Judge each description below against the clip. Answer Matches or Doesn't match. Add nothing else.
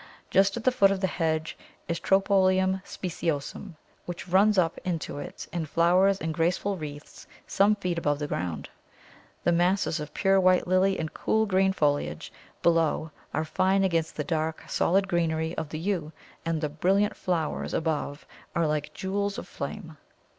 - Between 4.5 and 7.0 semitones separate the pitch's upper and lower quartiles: Doesn't match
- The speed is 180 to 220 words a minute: Doesn't match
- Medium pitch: Matches